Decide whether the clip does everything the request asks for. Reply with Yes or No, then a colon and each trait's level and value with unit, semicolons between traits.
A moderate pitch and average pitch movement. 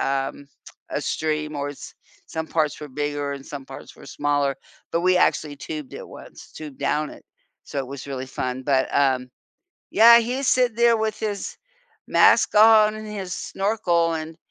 No: medium, 155 Hz; wide, 6.8 semitones